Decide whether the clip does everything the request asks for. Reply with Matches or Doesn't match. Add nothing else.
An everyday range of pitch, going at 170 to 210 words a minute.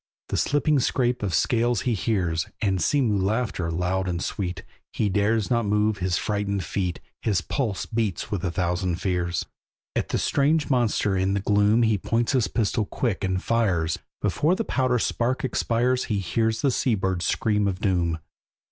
Matches